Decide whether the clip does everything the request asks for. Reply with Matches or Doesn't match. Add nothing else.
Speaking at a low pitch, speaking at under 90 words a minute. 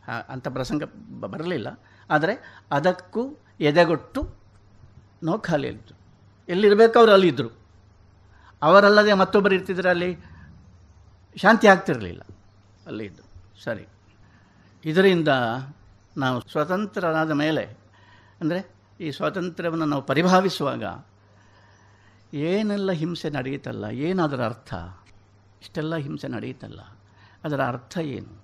Matches